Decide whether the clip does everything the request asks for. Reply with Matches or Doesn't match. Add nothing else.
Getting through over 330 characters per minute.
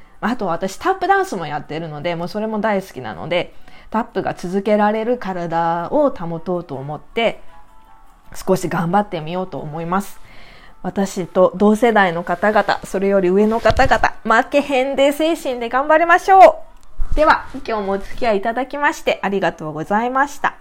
Matches